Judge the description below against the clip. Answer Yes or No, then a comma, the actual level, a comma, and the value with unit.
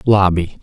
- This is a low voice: Yes, very low, 95 Hz